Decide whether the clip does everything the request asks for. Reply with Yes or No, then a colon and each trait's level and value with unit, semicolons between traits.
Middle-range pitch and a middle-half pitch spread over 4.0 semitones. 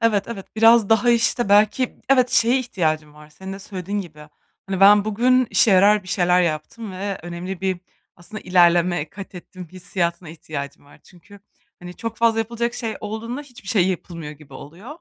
No: high, 195 Hz; average, 4.4 semitones